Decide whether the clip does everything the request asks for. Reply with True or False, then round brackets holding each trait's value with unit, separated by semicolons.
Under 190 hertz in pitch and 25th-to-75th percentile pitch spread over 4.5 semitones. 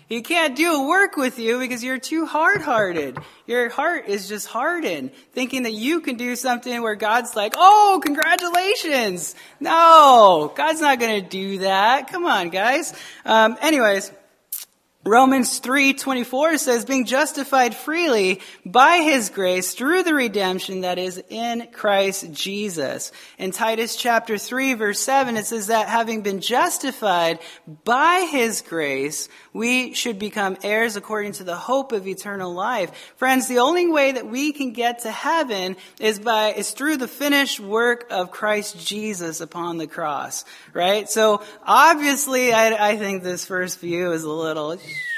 False (230 Hz; 5.2 semitones)